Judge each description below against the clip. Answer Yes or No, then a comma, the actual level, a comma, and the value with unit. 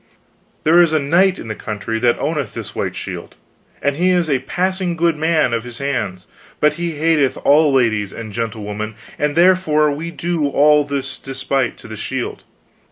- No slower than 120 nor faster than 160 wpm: No, average, 180 wpm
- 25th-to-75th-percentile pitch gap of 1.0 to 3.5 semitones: No, wide, 5.6 semitones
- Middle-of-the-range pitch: Yes, medium, 145 Hz